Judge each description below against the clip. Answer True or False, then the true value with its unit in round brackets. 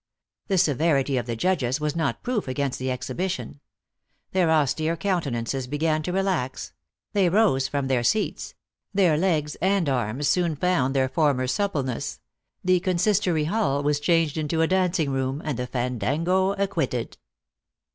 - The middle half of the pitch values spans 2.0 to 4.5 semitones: False (5.5 semitones)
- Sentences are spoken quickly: False (155 wpm)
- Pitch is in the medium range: True (155 Hz)